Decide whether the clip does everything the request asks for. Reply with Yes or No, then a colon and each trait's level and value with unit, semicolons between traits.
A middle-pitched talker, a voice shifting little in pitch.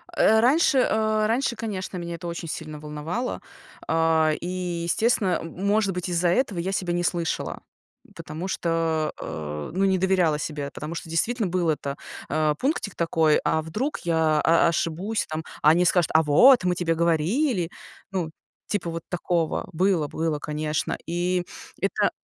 No: medium, 170 Hz; average, 3.3 semitones